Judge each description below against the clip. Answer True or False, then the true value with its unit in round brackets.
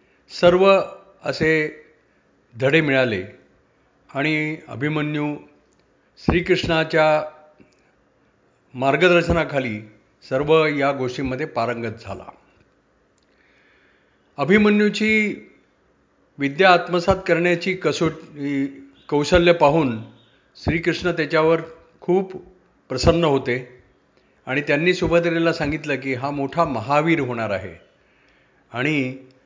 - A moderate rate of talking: False (75 wpm)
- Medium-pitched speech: True (150 Hz)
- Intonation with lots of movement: False (4.6 semitones)